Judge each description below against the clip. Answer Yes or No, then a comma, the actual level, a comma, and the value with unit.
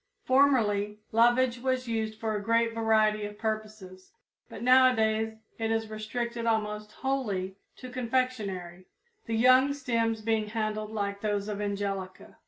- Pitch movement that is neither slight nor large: No, narrow, 2.2 semitones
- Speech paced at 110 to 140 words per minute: Yes, slow, 135 wpm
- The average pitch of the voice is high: Yes, high, 220 Hz